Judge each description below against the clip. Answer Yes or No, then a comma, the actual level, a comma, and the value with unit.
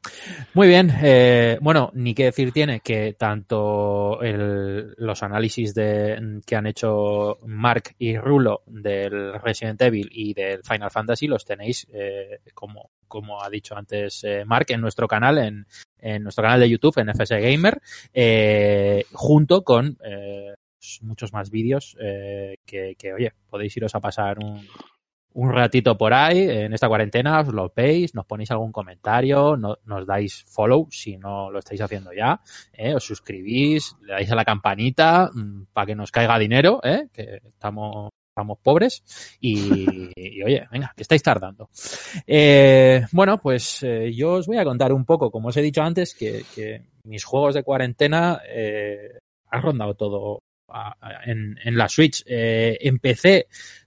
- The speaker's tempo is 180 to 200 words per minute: No, average, 165 wpm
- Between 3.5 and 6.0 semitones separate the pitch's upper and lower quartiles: Yes, average, 4.3 semitones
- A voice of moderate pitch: No, low, 110 Hz